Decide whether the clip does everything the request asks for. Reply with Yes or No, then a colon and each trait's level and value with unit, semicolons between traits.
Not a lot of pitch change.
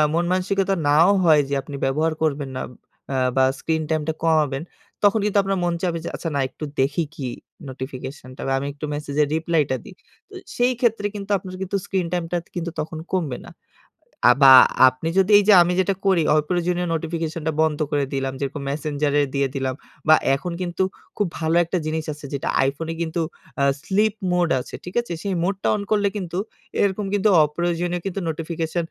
No: average, 3.9 semitones